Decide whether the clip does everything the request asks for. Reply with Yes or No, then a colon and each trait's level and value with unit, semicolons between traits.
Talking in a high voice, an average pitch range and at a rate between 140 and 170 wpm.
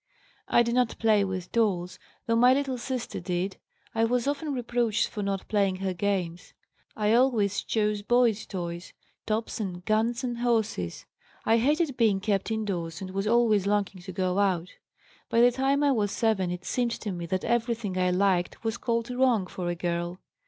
No: high, 210 Hz; average, 4.2 semitones; average, 180 wpm